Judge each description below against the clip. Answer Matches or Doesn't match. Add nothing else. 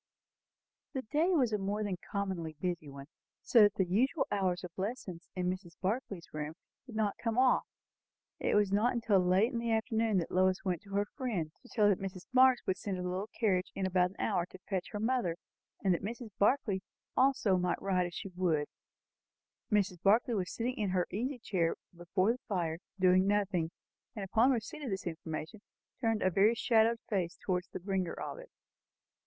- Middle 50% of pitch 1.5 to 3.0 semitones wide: Doesn't match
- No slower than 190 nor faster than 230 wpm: Matches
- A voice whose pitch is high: Matches